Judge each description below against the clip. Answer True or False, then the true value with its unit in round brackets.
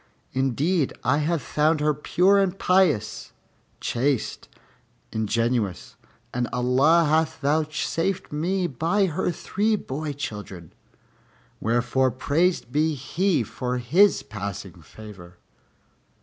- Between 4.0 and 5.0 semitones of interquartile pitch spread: False (5.6 semitones)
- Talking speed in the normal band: False (105 wpm)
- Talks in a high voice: False (145 Hz)